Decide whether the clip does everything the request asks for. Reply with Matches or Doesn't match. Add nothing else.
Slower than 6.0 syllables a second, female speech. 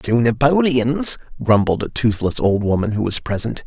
Doesn't match